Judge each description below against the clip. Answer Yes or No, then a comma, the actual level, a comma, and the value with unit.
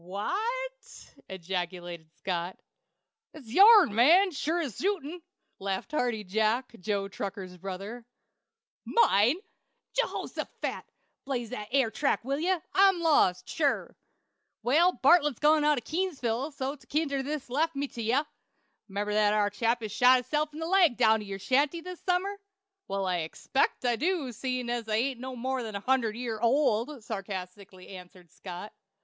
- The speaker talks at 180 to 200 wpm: No, average, 155 wpm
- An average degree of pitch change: No, wide, 6.6 semitones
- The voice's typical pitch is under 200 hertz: No, high, 245 Hz